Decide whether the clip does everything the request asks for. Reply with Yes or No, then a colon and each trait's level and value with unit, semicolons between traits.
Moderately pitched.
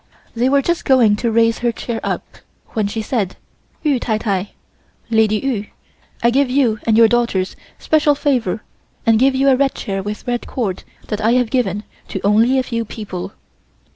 No: high, 230 Hz